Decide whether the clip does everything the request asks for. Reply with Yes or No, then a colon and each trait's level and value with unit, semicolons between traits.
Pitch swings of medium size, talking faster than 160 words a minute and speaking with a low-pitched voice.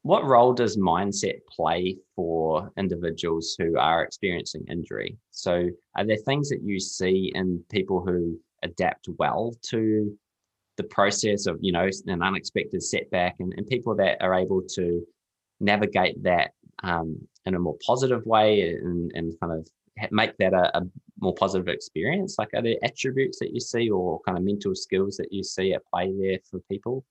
Yes: average, 3.3 semitones; average, 175 wpm; very low, 95 Hz